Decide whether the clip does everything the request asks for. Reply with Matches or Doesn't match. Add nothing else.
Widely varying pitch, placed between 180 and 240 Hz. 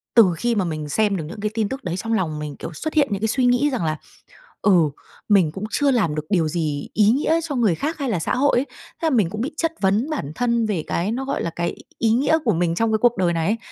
Matches